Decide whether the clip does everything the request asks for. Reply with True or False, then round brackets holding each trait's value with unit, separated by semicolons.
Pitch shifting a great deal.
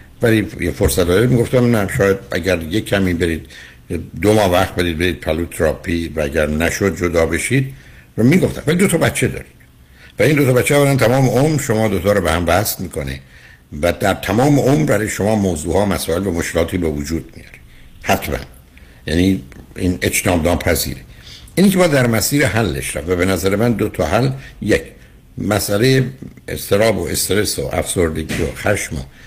True (6.2 semitones)